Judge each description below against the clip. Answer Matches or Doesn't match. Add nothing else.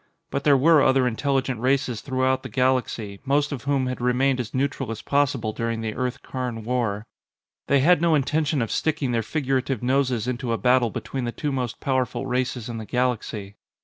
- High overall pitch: Doesn't match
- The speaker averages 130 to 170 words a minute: Doesn't match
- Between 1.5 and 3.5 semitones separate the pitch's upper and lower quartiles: Matches